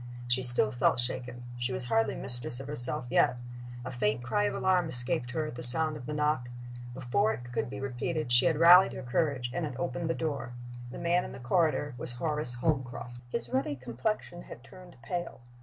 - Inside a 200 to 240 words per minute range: Yes, fast, 205 wpm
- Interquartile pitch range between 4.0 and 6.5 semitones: Yes, average, 4.4 semitones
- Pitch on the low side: Yes, low, 130 Hz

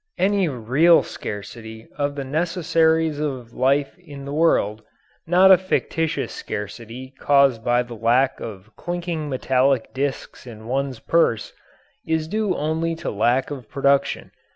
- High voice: No, medium, 140 Hz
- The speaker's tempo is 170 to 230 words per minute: No, slow, 135 wpm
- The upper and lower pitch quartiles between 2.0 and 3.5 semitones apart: No, average, 5.0 semitones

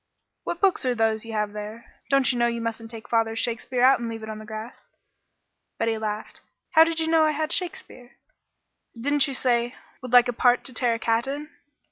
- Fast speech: Yes, fast, 220 wpm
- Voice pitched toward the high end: Yes, high, 235 Hz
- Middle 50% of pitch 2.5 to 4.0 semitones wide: Yes, average, 3.3 semitones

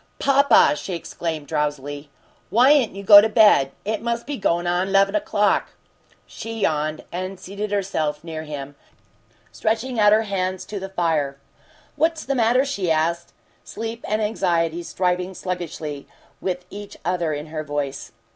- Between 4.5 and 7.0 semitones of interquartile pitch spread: Yes, average, 5.2 semitones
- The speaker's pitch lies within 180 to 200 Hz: Yes, medium, 185 Hz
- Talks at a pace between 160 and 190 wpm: No, average, 150 wpm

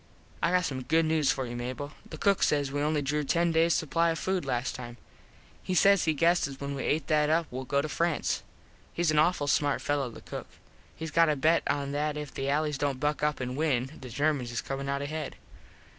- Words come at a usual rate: No, fast, 225 wpm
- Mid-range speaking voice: Yes, medium, 150 Hz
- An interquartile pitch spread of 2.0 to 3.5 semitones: Yes, average, 2.8 semitones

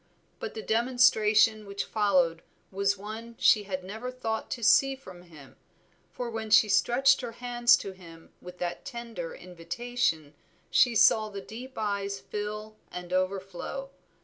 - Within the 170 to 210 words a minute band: No, average, 150 wpm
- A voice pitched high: Yes, high, 210 Hz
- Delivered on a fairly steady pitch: No, average, 4.1 semitones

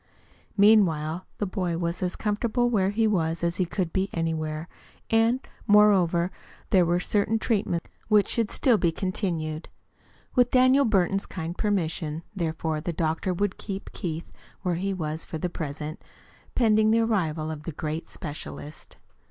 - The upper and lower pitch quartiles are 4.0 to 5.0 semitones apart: Yes, average, 4.4 semitones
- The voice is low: No, medium, 180 Hz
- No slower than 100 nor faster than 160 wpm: Yes, average, 150 wpm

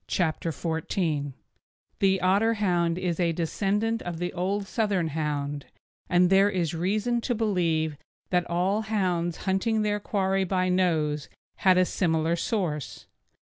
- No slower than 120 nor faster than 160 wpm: Yes, average, 140 wpm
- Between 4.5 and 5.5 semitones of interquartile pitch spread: No, average, 3.3 semitones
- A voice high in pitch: No, medium, 180 Hz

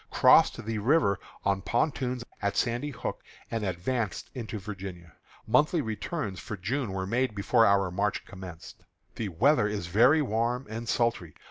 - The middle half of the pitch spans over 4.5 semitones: No, average, 4.1 semitones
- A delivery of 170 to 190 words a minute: No, average, 150 wpm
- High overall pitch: No, low, 110 Hz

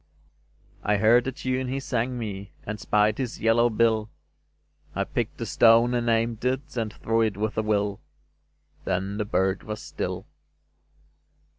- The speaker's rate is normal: Yes, average, 155 wpm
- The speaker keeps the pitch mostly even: Yes, narrow, 2.3 semitones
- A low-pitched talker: Yes, low, 115 Hz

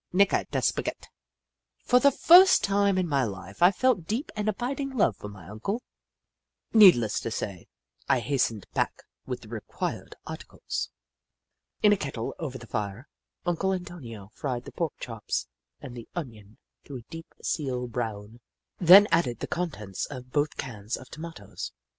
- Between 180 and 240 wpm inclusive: No, average, 160 wpm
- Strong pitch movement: Yes, wide, 8.8 semitones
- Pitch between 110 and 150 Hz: Yes, low, 135 Hz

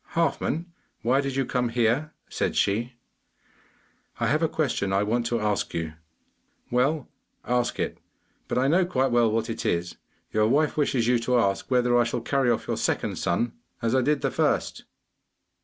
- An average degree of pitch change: Yes, average, 3.1 semitones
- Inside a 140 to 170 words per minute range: No, average, 180 wpm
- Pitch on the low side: Yes, low, 125 Hz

